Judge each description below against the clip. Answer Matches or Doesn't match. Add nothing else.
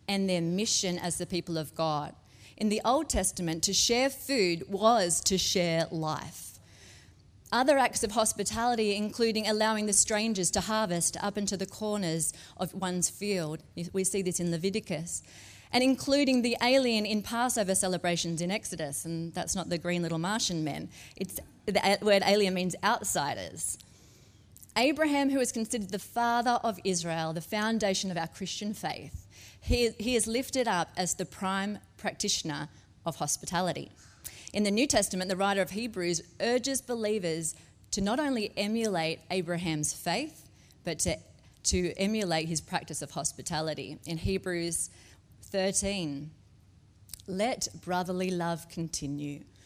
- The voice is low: Doesn't match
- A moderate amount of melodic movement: Matches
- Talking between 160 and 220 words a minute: Doesn't match